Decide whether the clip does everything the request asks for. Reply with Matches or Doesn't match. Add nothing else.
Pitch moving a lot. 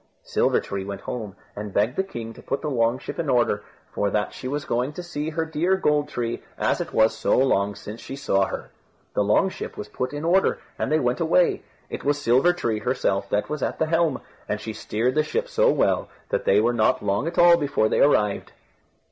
Matches